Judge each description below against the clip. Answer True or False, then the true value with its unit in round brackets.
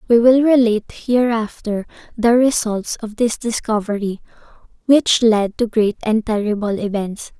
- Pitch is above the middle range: True (225 Hz)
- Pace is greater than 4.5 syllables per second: False (4.4 syllables/s)